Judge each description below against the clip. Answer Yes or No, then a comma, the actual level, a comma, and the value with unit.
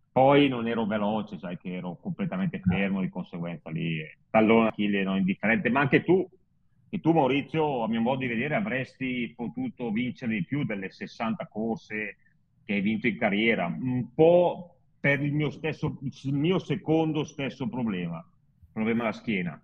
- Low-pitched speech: Yes, low, 130 Hz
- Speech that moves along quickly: Yes, fast, 175 wpm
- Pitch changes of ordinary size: No, wide, 6.9 semitones